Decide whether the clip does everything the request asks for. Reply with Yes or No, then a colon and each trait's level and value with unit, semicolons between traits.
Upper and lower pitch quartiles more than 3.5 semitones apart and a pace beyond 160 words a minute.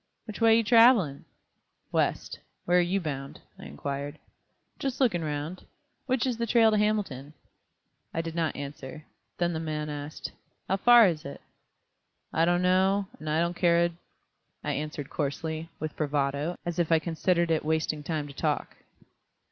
Yes: average, 4.0 semitones; average, 170 wpm